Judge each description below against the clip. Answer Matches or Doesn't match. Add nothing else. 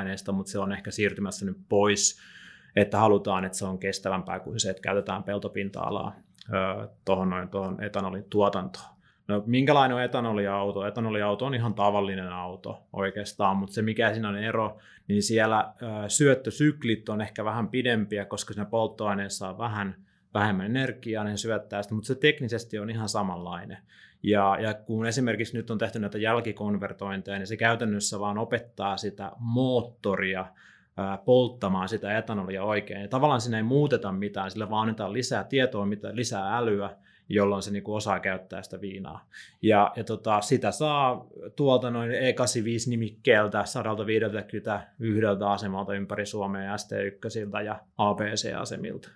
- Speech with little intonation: Matches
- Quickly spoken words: Doesn't match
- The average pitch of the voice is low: Matches